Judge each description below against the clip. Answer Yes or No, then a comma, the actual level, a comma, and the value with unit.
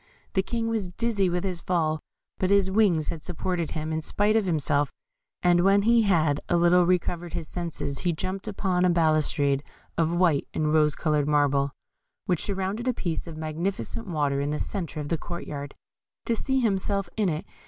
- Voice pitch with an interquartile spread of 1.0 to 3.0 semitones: No, average, 3.9 semitones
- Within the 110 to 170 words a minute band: No, average, 190 wpm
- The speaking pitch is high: No, medium, 175 Hz